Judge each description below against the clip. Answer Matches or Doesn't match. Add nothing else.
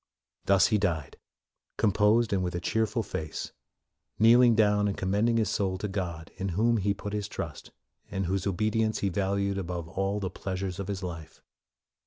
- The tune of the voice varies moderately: Doesn't match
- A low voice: Matches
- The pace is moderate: Matches